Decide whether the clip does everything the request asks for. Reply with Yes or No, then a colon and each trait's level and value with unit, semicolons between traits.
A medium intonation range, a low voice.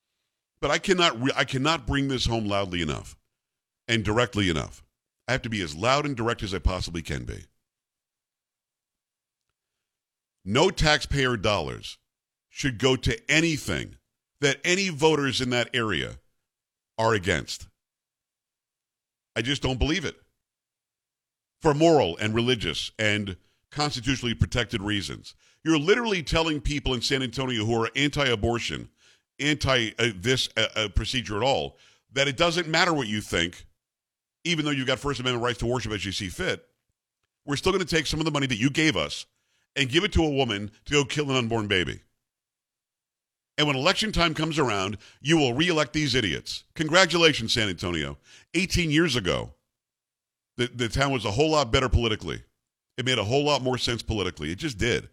No: wide, 5.7 semitones; low, 130 Hz